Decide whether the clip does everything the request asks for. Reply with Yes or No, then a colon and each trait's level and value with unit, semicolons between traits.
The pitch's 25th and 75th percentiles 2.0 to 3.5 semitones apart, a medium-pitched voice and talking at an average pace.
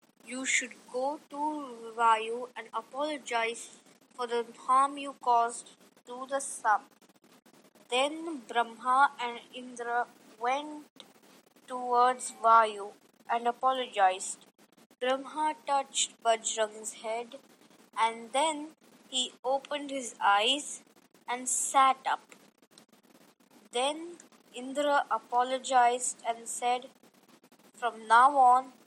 No: narrow, 2.6 semitones; very high, 250 Hz; average, 95 wpm